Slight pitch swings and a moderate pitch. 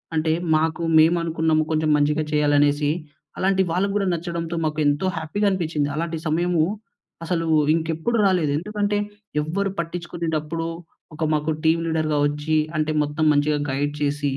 Yes: narrow, 2.2 semitones; medium, 160 Hz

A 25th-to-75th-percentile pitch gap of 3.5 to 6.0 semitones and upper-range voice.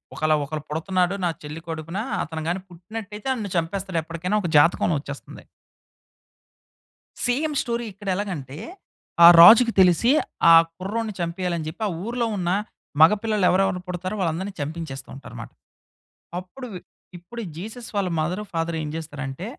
No: average, 4.1 semitones; medium, 180 Hz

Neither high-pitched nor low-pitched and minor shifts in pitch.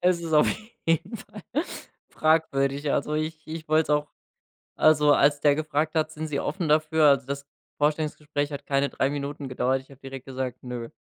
Yes: medium, 150 Hz; narrow, 2.1 semitones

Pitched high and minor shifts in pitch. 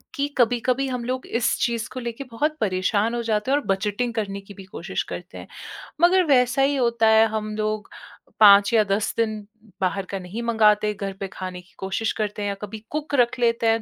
No: high, 220 Hz; average, 3.1 semitones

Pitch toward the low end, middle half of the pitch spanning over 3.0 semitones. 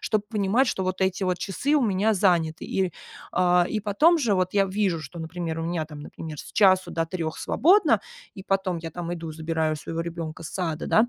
No: medium, 180 Hz; average, 3.4 semitones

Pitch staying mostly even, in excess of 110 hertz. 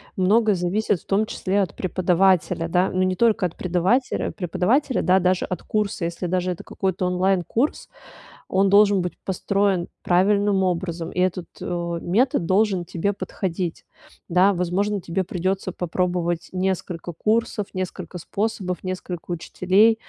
Yes: narrow, 2.2 semitones; medium, 185 Hz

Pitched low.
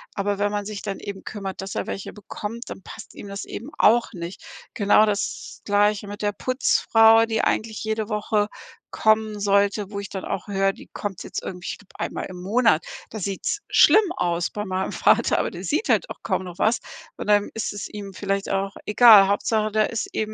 No: high, 205 Hz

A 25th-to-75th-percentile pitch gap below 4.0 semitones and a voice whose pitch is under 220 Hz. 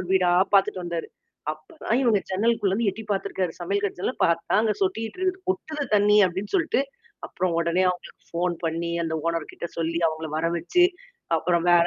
Yes: average, 3.6 semitones; medium, 185 Hz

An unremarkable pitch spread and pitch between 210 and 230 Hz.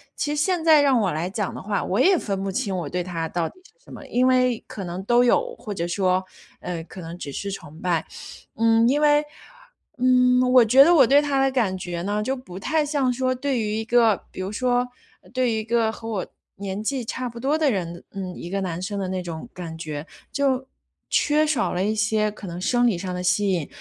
No: wide, 5.8 semitones; high, 215 Hz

